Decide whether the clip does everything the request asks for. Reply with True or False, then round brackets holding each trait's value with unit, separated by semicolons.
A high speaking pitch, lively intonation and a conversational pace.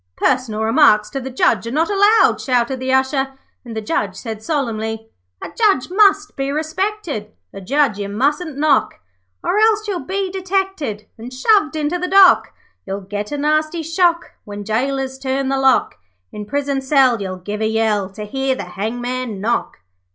True (265 Hz; 6.2 semitones; 175 wpm)